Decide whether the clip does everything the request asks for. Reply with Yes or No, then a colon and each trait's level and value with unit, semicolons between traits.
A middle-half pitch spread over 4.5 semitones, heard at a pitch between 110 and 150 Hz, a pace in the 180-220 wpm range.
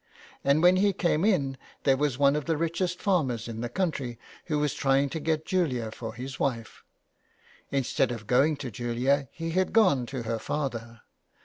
Yes: average, 5.0 semitones; medium, 140 Hz; average, 185 wpm